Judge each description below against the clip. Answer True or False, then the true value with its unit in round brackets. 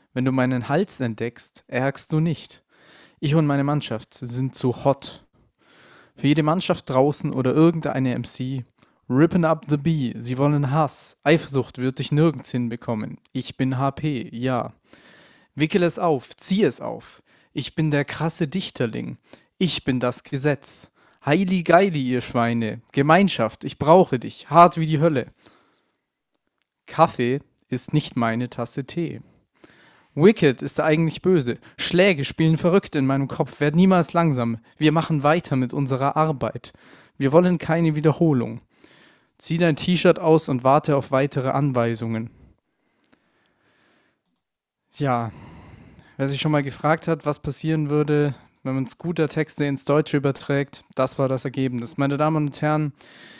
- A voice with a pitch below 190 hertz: True (140 Hz)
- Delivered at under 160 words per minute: True (145 wpm)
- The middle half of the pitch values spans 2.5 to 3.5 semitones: False (3.9 semitones)